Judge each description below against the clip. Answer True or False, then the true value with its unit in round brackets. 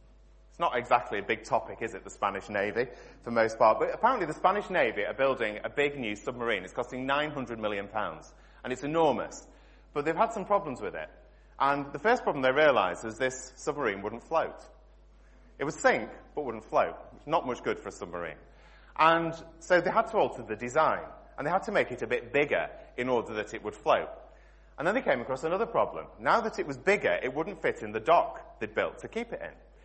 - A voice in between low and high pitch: True (145 Hz)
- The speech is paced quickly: True (220 wpm)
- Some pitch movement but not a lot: False (6.7 semitones)